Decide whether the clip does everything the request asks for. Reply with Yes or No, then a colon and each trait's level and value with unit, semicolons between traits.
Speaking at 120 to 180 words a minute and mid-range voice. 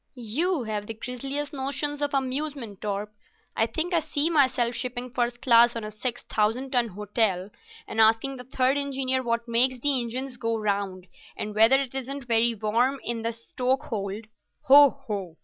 No: average, 165 wpm; high, 245 Hz